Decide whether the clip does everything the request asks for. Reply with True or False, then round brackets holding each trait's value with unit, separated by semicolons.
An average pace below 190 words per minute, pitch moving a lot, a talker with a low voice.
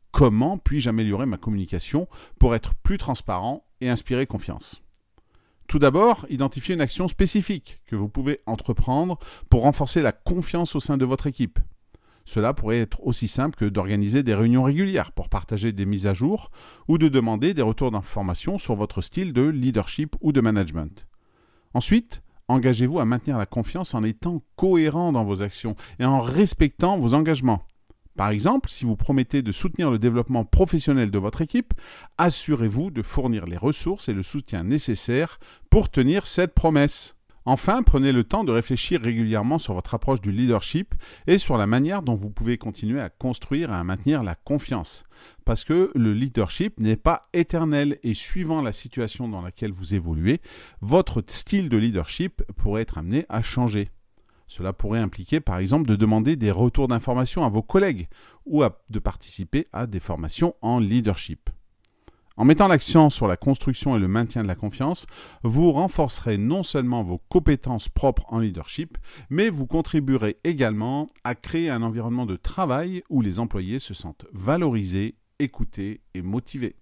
True (170 wpm; 5.7 semitones; 120 Hz)